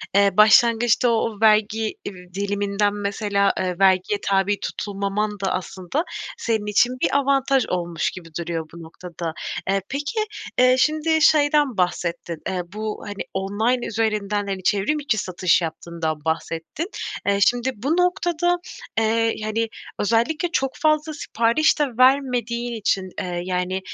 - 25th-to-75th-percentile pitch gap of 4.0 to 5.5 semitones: Yes, average, 4.8 semitones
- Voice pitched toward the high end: Yes, high, 210 Hz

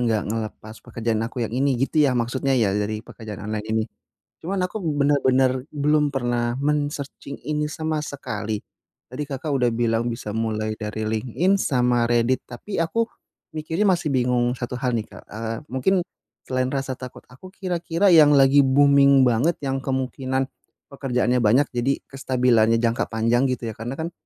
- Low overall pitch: Yes, low, 130 Hz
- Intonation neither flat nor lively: Yes, average, 3.5 semitones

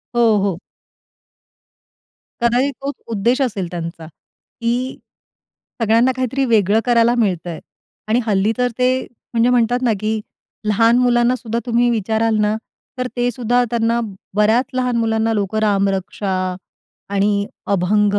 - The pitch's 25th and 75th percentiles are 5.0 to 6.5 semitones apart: No, average, 2.9 semitones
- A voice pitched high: Yes, high, 225 Hz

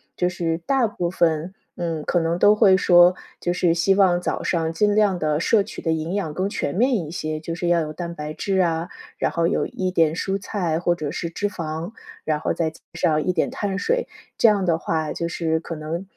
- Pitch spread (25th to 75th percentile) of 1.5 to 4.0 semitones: Yes, average, 2.8 semitones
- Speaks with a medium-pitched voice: Yes, medium, 170 Hz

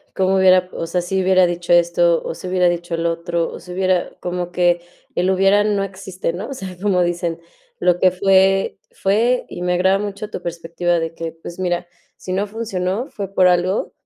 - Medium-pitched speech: Yes, medium, 180 Hz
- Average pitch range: No, narrow, 1.8 semitones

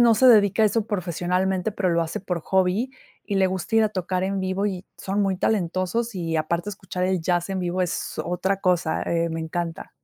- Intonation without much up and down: Yes, narrow, 2.3 semitones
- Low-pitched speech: No, medium, 185 Hz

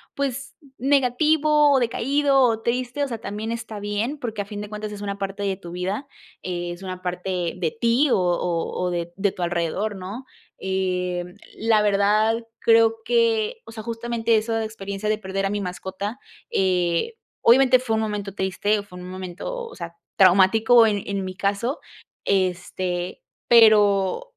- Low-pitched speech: No, high, 205 Hz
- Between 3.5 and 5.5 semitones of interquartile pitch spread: Yes, average, 3.9 semitones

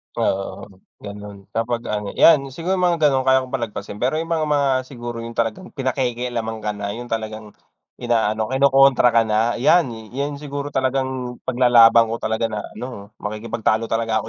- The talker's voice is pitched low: Yes, low, 120 Hz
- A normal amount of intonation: Yes, average, 3.3 semitones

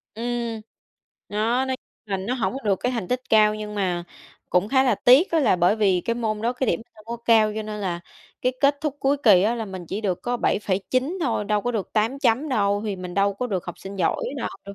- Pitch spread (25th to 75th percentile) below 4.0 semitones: Yes, average, 3.6 semitones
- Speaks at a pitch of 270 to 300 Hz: No, high, 215 Hz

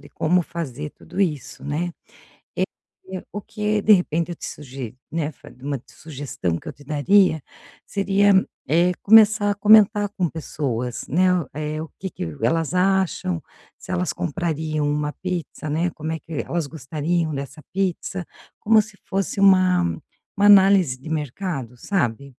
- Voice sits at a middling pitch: Yes, medium, 170 Hz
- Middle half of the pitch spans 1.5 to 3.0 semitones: No, average, 4.5 semitones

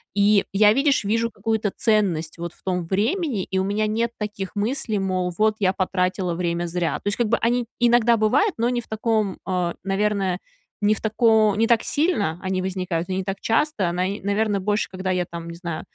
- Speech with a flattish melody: No, average, 3.2 semitones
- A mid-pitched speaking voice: No, high, 205 Hz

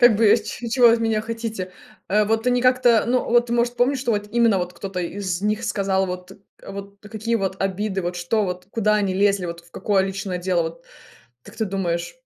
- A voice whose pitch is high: Yes, high, 205 Hz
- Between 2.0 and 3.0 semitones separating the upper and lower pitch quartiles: No, average, 3.6 semitones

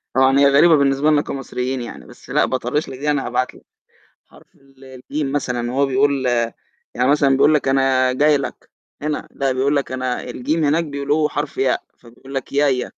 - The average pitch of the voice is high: No, low, 135 Hz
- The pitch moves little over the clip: Yes, narrow, 2.0 semitones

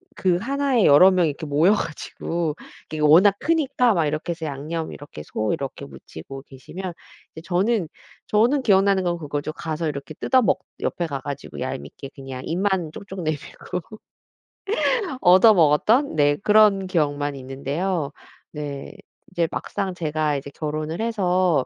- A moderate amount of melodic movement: Yes, average, 4.8 semitones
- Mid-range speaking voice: Yes, medium, 165 Hz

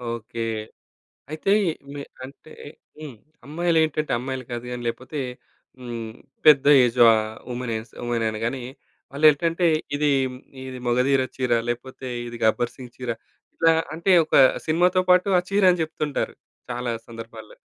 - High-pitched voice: No, low, 130 Hz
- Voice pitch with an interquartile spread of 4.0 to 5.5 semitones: Yes, average, 4.6 semitones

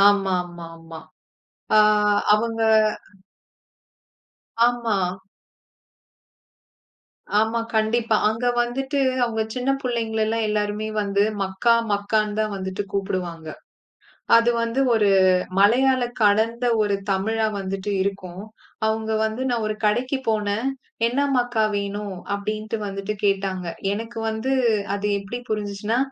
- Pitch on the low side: No, high, 215 Hz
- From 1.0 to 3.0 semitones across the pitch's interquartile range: Yes, narrow, 2.6 semitones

